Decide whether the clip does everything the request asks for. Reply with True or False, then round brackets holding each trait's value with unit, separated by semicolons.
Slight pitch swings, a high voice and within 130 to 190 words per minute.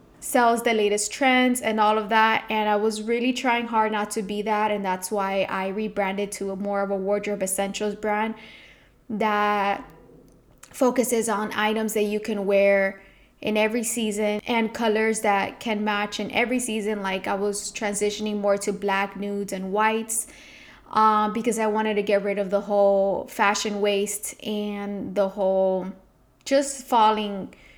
True (1.6 semitones; 210 Hz; 165 wpm)